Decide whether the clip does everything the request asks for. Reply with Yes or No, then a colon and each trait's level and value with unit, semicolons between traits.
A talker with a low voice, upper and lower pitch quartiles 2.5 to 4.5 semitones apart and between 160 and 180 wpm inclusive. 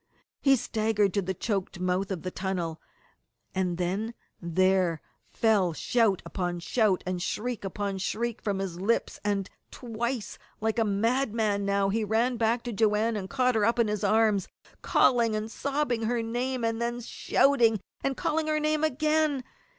No: high, 220 Hz; average, 3.6 semitones; average, 165 wpm